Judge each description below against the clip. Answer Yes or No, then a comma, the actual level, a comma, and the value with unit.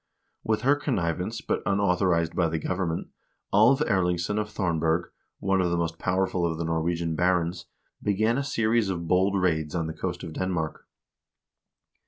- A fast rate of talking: No, average, 165 wpm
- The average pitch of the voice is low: Yes, very low, 90 Hz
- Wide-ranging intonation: No, average, 3.1 semitones